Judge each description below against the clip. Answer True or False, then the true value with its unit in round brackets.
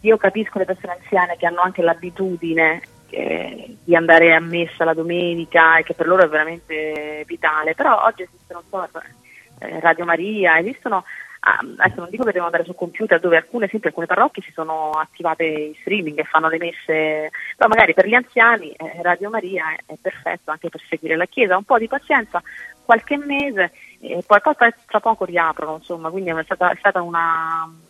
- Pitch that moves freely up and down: False (3.4 semitones)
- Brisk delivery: True (195 wpm)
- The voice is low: False (175 Hz)